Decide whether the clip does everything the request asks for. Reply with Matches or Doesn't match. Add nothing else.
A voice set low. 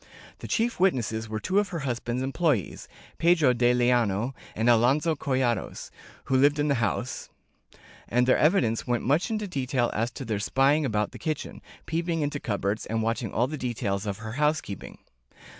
Matches